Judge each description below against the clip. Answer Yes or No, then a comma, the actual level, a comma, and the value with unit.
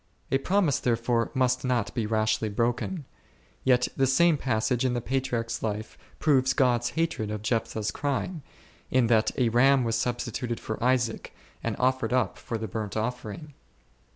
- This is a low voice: Yes, low, 120 Hz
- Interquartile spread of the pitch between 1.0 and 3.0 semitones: Yes, average, 2.7 semitones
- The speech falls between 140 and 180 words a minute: Yes, average, 155 wpm